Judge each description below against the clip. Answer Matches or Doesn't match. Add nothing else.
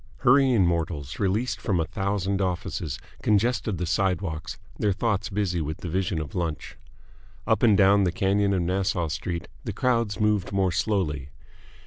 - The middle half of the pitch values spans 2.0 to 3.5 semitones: Matches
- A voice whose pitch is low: Matches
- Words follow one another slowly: Doesn't match